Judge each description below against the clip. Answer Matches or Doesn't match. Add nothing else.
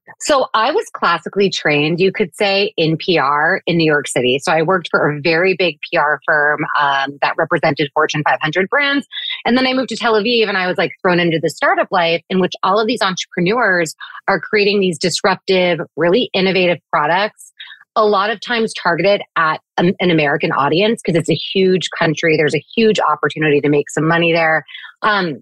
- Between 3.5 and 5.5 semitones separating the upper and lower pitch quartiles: Matches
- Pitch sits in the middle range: Matches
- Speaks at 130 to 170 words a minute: Doesn't match